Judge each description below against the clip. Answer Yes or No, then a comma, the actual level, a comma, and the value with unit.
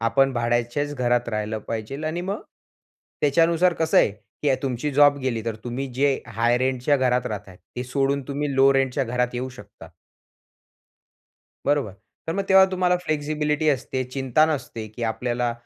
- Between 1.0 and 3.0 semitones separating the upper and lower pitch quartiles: No, average, 3.4 semitones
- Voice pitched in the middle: No, low, 130 Hz